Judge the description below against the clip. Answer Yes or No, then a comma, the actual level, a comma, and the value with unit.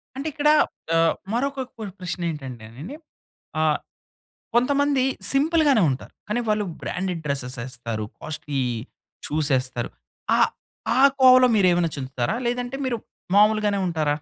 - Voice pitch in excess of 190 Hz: No, medium, 185 Hz